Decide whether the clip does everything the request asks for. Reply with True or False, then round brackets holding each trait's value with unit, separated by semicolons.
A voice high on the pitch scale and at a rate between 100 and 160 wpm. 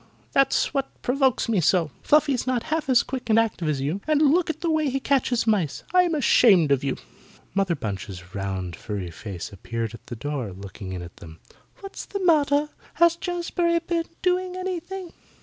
False (240 Hz; 185 wpm)